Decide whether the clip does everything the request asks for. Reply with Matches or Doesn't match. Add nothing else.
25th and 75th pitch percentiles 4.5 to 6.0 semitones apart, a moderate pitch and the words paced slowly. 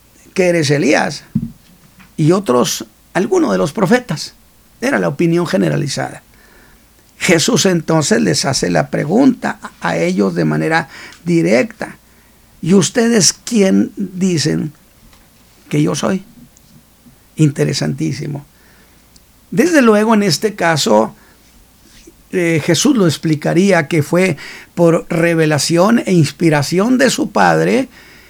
Matches